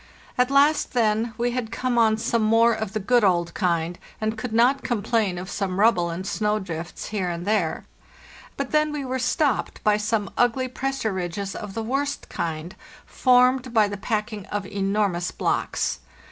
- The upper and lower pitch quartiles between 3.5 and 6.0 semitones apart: Yes, average, 4.2 semitones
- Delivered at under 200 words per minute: Yes, average, 175 wpm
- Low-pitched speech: No, high, 220 Hz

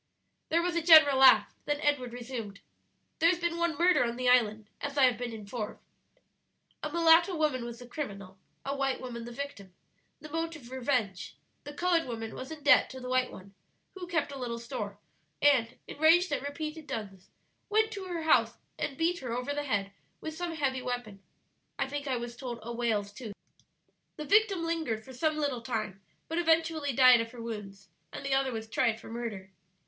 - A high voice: Yes, very high, 260 Hz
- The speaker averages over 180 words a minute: Yes, average, 195 wpm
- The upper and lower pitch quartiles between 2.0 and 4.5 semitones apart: No, average, 5.3 semitones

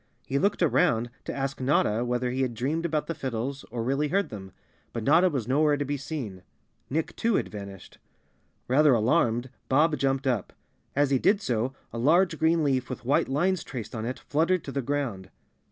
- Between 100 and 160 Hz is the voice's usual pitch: Yes, low, 135 Hz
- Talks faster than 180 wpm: Yes, average, 195 wpm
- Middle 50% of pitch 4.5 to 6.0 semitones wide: No, average, 4.0 semitones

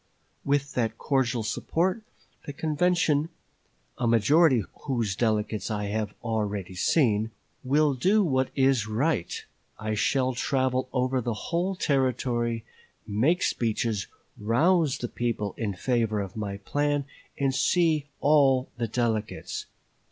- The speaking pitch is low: Yes, low, 125 Hz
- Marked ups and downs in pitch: No, average, 4.8 semitones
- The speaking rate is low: Yes, slow, 125 wpm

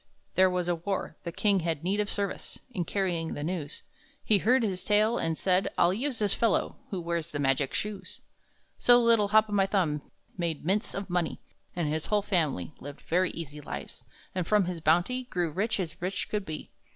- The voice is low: No, medium, 185 Hz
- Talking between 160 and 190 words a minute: No, average, 200 wpm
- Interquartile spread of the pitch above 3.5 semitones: Yes, average, 4.0 semitones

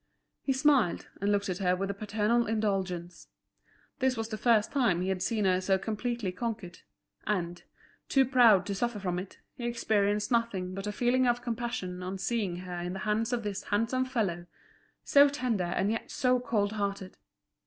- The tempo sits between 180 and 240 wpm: Yes, average, 185 wpm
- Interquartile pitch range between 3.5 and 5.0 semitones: Yes, average, 4.1 semitones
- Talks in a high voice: Yes, high, 210 Hz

